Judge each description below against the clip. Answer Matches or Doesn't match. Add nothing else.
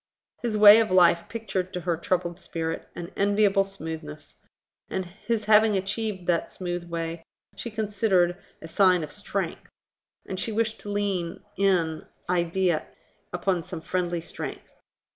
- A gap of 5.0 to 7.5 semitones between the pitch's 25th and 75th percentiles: Doesn't match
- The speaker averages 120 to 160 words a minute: Matches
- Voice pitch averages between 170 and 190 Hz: Matches